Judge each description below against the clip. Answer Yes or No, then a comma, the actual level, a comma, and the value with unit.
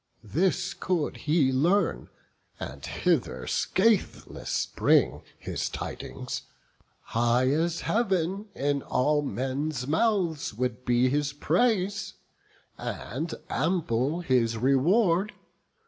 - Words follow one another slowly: Yes, slow, 95 wpm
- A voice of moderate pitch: Yes, medium, 150 Hz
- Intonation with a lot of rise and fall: Yes, wide, 6.2 semitones